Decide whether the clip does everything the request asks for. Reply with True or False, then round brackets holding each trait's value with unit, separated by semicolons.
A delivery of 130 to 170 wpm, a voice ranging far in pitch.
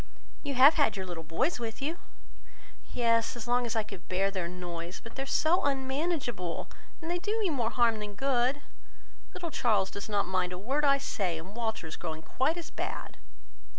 False (200 wpm; 6.7 semitones)